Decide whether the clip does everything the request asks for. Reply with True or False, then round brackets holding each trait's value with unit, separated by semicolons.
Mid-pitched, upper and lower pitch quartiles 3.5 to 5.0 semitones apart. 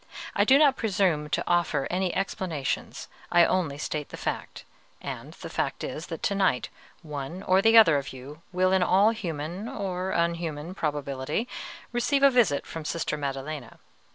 True (175 Hz; 4.6 semitones)